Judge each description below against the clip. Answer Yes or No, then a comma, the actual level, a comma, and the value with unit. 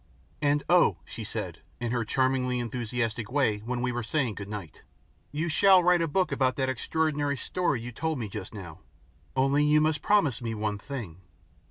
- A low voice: Yes, low, 130 Hz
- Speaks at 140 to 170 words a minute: No, average, 180 wpm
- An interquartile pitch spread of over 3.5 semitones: Yes, average, 4.8 semitones